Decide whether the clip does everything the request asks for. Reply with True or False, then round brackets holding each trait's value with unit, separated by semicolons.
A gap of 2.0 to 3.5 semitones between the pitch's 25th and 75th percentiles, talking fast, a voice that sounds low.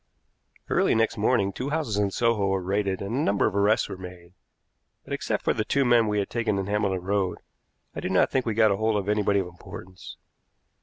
True (2.5 semitones; 210 wpm; 105 Hz)